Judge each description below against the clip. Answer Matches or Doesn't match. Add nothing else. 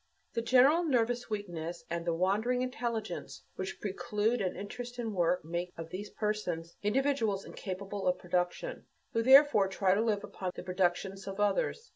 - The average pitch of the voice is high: Matches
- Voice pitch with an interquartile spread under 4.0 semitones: Doesn't match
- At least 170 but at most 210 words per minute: Doesn't match